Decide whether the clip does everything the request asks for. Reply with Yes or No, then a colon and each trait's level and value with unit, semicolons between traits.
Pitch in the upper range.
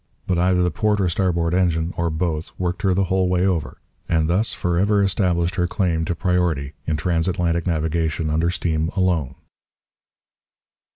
No: very low, 85 Hz